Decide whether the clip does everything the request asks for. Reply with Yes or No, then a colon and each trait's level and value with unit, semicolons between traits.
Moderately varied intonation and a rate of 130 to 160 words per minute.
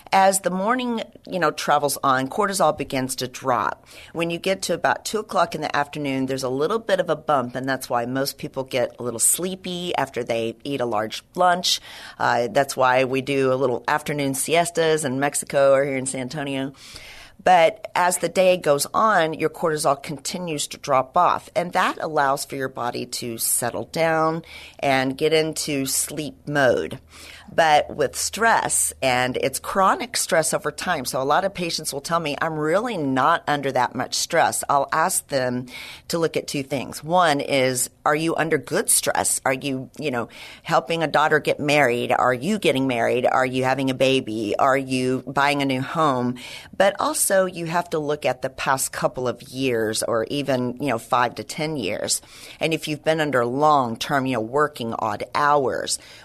No: average, 3.7 semitones; average, 190 wpm